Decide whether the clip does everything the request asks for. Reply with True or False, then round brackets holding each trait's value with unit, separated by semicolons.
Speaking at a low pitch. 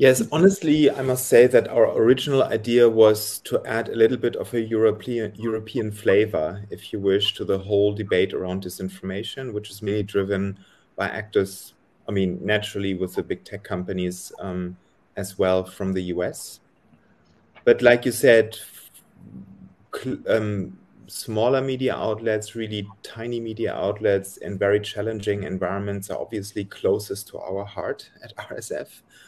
True (105 Hz)